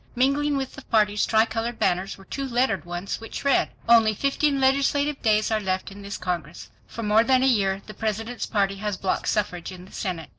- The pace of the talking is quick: Yes, fast, 210 wpm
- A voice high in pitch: Yes, high, 220 Hz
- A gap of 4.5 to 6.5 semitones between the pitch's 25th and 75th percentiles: Yes, average, 4.9 semitones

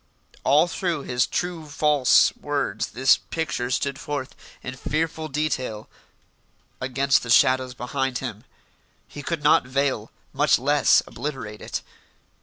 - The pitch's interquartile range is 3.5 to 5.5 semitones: No, average, 2.8 semitones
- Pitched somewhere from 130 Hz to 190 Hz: Yes, medium, 140 Hz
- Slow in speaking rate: Yes, slow, 125 wpm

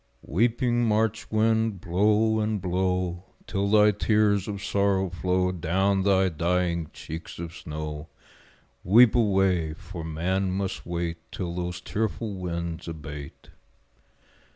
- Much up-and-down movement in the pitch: No, average, 3.5 semitones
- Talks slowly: Yes, slow, 120 wpm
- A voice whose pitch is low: Yes, very low, 95 Hz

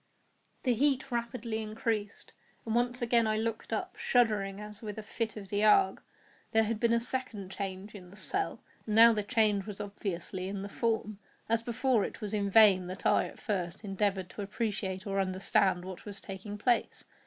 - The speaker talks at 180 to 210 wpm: Yes, average, 190 wpm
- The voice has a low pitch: No, high, 210 Hz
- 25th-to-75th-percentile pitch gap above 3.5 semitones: No, average, 2.7 semitones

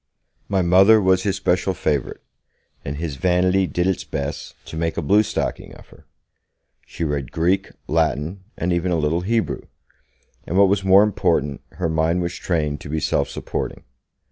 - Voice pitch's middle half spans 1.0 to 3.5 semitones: Yes, average, 3.2 semitones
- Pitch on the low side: Yes, very low, 90 Hz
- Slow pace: No, average, 170 wpm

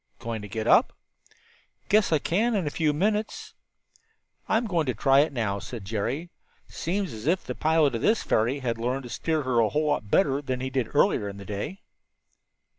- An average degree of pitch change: No, wide, 6.3 semitones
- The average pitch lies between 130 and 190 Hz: Yes, low, 135 Hz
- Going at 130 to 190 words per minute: No, average, 200 wpm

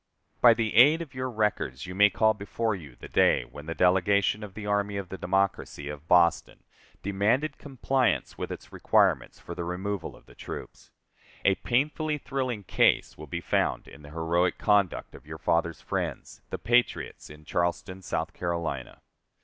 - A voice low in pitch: Yes, very low, 95 Hz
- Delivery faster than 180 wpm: No, average, 175 wpm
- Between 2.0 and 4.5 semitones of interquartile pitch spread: No, average, 5.0 semitones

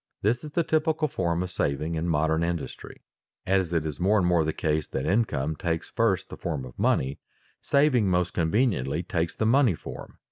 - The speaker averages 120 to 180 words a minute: No, average, 200 wpm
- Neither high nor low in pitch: No, very low, 90 Hz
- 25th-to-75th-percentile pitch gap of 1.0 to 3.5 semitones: No, wide, 5.5 semitones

